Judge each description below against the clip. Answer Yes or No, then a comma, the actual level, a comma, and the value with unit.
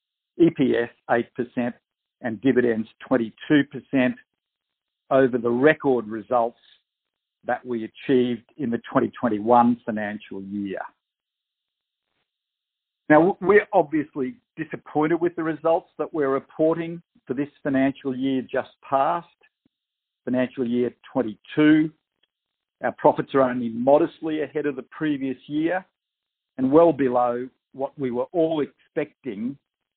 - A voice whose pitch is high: No, low, 135 Hz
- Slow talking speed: Yes, slow, 110 wpm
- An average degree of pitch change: Yes, average, 4.3 semitones